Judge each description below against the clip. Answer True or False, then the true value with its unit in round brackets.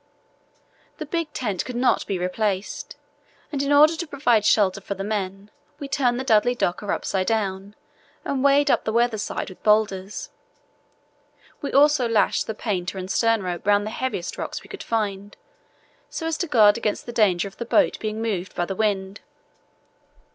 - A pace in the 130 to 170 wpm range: False (180 wpm)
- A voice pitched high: True (215 Hz)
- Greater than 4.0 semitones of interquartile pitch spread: True (4.7 semitones)